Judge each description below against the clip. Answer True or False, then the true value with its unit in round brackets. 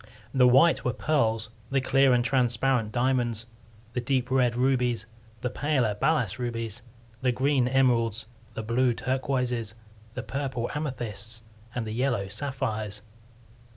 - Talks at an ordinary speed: False (130 wpm)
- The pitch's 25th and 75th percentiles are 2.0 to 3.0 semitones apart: True (2.6 semitones)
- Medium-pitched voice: False (125 Hz)